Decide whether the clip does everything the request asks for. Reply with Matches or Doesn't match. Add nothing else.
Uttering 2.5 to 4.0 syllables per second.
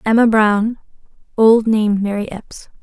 Matches